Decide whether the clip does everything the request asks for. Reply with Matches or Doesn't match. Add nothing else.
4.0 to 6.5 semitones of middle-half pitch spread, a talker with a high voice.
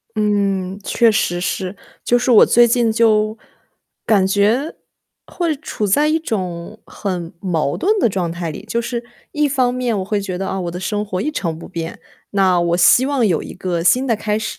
Matches